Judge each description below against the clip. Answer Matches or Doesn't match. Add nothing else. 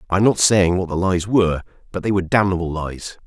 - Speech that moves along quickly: Matches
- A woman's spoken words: Doesn't match